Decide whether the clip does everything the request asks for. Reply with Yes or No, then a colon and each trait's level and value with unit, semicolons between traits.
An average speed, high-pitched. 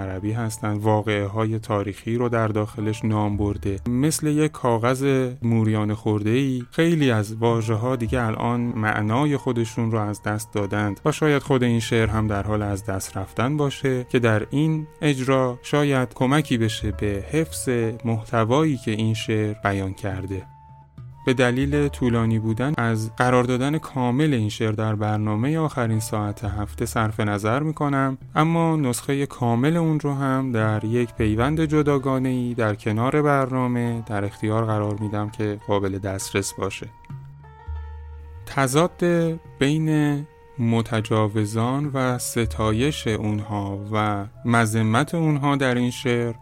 No: average, 140 wpm; low, 115 Hz